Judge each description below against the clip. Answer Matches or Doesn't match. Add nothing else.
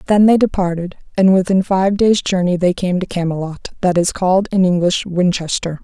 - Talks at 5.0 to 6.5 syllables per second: Matches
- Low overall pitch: Doesn't match